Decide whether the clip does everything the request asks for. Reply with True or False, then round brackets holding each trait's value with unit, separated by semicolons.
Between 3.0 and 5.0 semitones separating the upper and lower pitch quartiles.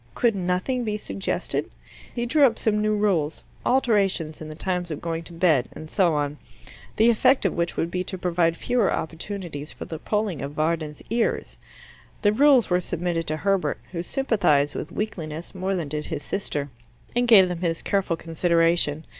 True (4.7 semitones)